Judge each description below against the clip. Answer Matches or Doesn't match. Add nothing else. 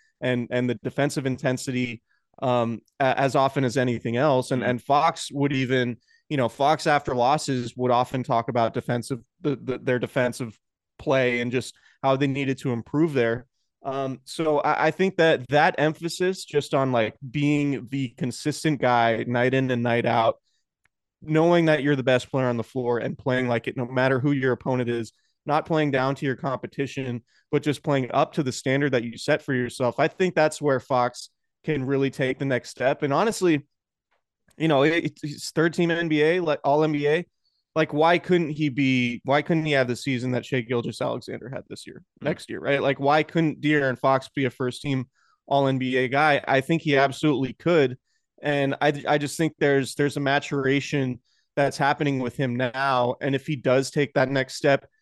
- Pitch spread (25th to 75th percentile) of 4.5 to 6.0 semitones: Doesn't match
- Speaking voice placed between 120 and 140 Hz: Matches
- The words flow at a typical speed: Matches